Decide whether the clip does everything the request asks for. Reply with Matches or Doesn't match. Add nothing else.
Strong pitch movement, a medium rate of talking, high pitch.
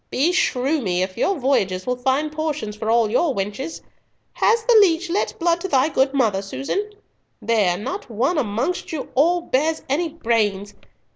Matches